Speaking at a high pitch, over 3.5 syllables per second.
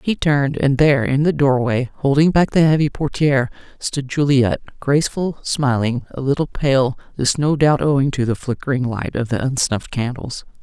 No: medium, 140 Hz; 5.2 syllables/s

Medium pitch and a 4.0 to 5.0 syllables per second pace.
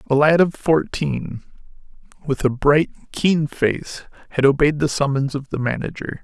Yes: medium, 145 Hz; 4.5 syllables/s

